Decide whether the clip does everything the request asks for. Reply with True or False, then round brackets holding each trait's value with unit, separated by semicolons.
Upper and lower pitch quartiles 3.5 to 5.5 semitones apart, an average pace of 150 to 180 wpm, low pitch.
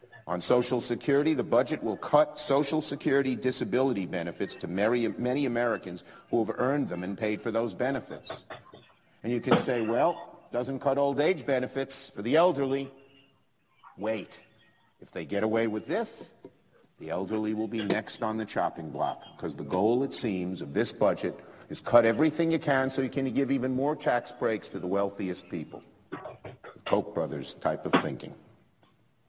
True (3.9 semitones; 170 wpm; 125 Hz)